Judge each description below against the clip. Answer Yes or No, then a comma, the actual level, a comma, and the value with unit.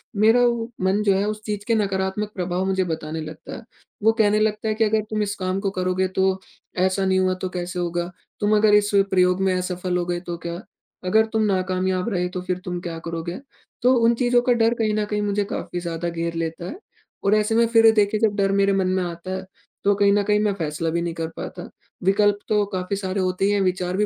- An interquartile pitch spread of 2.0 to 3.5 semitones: Yes, average, 2.7 semitones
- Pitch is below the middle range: No, high, 190 Hz